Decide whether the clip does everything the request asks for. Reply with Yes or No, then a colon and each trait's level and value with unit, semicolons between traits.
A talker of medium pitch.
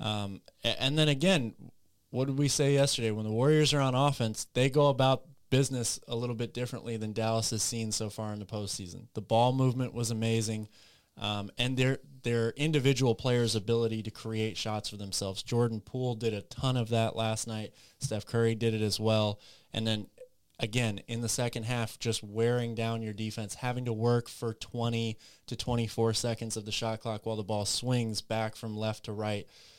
No: low, 115 Hz